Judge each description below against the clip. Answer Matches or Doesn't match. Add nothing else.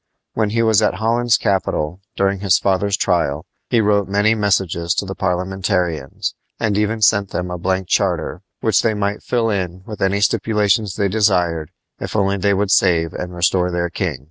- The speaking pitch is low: Matches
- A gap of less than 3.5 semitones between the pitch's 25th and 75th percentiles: Matches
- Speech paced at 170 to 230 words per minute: Matches